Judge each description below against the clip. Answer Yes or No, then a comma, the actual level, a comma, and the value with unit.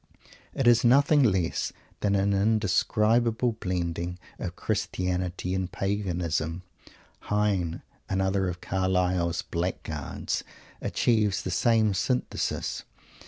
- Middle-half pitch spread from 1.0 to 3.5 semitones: Yes, average, 3.1 semitones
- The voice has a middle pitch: No, very low, 95 Hz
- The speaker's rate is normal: No, slow, 95 wpm